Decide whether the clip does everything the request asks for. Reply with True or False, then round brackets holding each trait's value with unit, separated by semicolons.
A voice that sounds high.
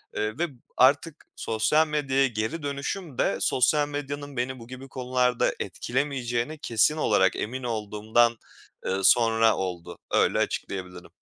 False (125 Hz)